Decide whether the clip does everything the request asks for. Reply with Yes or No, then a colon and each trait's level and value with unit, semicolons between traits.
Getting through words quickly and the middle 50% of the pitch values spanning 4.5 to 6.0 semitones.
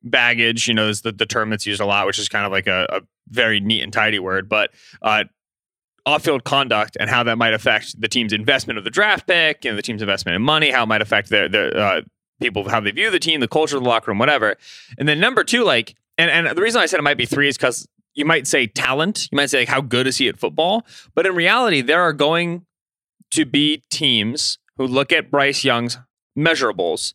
Yes: fast, 250 wpm; average, 5.1 semitones